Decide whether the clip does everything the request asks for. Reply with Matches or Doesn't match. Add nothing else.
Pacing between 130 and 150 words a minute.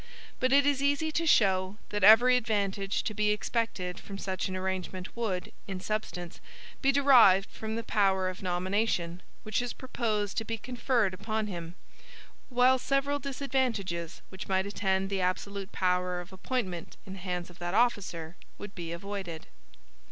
Doesn't match